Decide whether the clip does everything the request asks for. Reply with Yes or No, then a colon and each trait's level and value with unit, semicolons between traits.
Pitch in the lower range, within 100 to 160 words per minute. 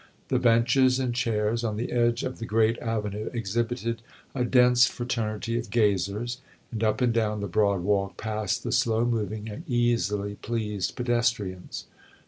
Yes: low, 115 Hz; average, 155 wpm